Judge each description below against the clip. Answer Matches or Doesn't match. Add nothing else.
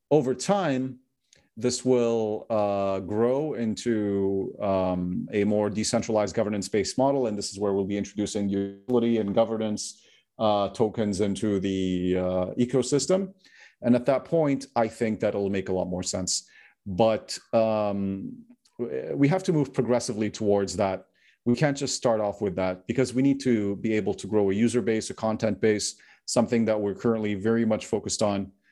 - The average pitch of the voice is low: Matches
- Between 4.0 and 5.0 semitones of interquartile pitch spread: Doesn't match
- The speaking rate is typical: Matches